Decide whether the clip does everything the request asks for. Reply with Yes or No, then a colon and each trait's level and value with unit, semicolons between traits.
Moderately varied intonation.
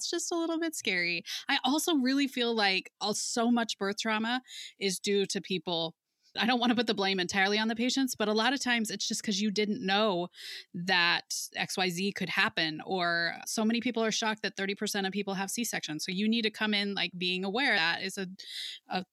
Yes: average, 3.5 semitones